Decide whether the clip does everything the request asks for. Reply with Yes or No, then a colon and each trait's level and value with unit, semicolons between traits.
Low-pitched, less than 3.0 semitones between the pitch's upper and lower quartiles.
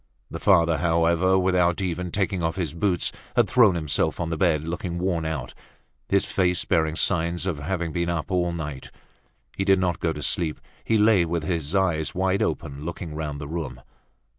Yes: very low, 85 Hz; narrow, 2.6 semitones